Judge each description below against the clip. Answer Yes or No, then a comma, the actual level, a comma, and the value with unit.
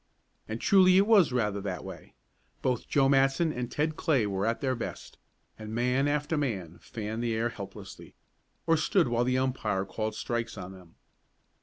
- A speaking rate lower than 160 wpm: No, average, 175 wpm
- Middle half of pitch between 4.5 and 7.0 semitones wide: Yes, average, 4.9 semitones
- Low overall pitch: Yes, low, 120 Hz